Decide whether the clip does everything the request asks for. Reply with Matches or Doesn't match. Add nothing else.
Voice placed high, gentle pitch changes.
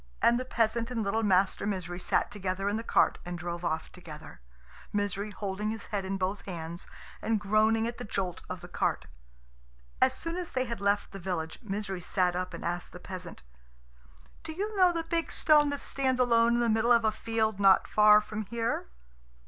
Doesn't match